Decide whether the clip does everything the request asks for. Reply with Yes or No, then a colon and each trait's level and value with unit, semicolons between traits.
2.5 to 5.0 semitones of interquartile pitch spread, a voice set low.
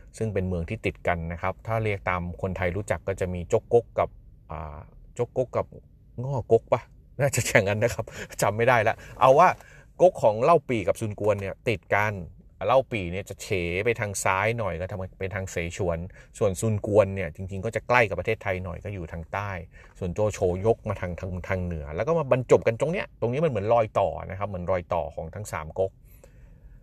Yes: average, 3.9 semitones; low, 100 Hz